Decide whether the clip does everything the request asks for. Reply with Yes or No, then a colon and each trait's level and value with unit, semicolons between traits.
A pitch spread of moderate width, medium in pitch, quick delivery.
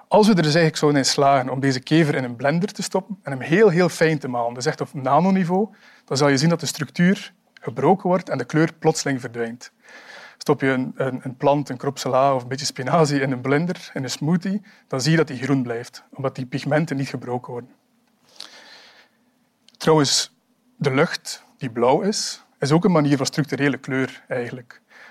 No: wide, 6.2 semitones; medium, 150 Hz; fast, 205 wpm